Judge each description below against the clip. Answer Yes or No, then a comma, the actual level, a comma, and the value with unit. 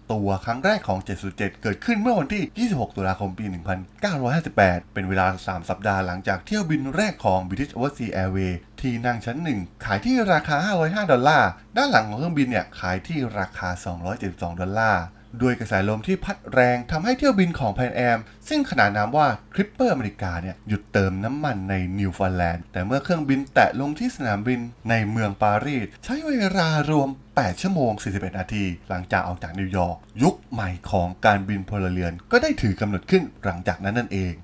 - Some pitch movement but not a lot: No, wide, 7.0 semitones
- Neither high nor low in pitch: No, low, 105 Hz